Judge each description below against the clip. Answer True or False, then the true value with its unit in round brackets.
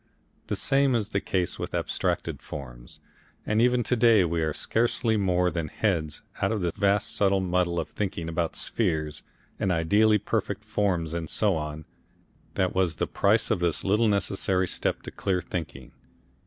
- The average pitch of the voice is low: True (95 Hz)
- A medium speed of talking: True (170 wpm)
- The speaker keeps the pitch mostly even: False (4.0 semitones)